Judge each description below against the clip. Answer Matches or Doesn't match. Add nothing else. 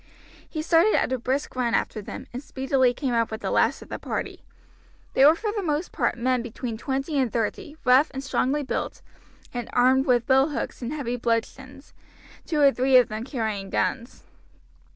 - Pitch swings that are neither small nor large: Matches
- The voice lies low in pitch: Doesn't match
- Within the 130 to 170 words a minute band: Doesn't match